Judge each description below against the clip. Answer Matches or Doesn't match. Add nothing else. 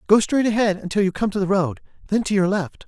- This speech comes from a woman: Doesn't match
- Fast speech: Matches